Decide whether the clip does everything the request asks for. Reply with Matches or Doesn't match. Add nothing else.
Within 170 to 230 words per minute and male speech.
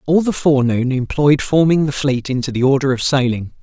Matches